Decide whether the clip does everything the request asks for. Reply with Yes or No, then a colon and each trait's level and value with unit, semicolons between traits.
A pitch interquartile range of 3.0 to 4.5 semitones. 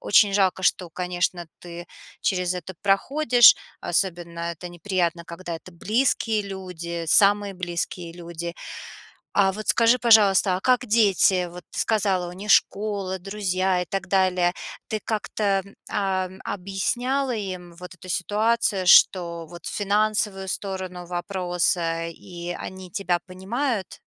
No: narrow, 2.6 semitones